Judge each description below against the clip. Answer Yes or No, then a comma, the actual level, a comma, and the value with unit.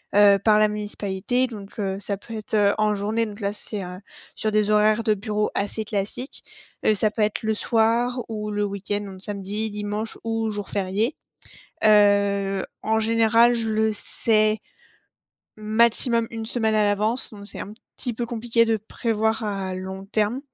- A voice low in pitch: No, high, 215 Hz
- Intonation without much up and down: Yes, narrow, 1.6 semitones